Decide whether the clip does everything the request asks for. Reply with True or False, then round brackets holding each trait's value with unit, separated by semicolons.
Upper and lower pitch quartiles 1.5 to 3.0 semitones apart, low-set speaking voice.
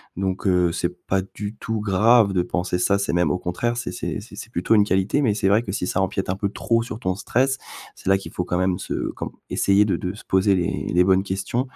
True (2.4 semitones; 95 Hz)